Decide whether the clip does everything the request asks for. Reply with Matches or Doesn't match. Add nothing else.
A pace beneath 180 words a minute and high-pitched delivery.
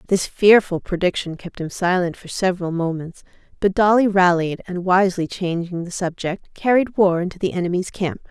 Doesn't match